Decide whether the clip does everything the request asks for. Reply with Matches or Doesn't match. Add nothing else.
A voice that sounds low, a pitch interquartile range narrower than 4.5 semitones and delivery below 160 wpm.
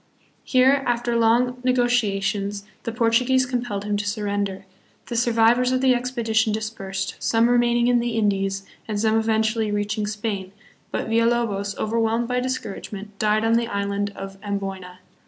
Doesn't match